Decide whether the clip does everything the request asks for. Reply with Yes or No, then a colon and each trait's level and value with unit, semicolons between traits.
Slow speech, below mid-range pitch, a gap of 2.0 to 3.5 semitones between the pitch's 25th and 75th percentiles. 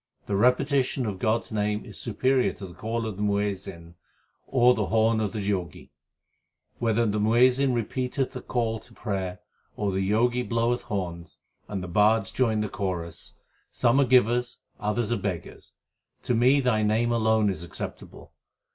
No: average, 170 wpm; low, 110 Hz; average, 3.1 semitones